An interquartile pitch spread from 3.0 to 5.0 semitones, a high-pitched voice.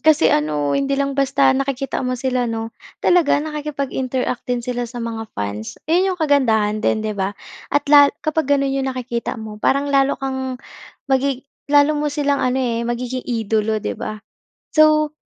Yes: average, 3.7 semitones; very high, 260 Hz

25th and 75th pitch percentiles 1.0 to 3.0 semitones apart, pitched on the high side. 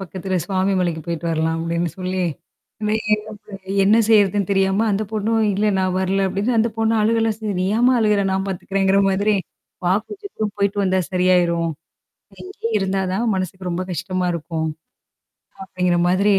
Yes: narrow, 2.6 semitones; high, 195 Hz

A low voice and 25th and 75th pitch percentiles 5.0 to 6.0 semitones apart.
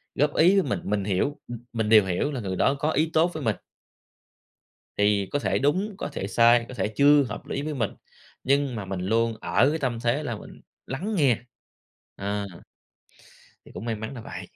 Yes: low, 120 Hz; wide, 5.5 semitones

